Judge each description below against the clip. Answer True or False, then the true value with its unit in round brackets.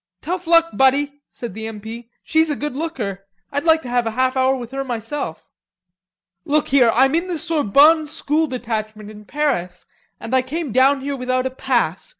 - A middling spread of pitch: True (4.5 semitones)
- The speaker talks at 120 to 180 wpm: False (190 wpm)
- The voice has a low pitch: False (265 Hz)